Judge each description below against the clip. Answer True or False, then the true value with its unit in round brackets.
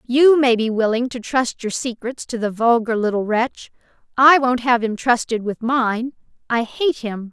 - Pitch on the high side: True (240 Hz)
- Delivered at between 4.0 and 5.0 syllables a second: True (4.4 syllables/s)